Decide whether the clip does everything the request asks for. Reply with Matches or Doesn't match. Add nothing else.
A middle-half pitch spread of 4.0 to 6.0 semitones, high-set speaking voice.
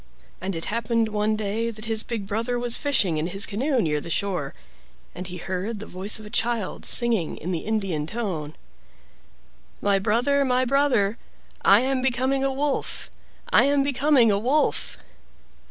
Matches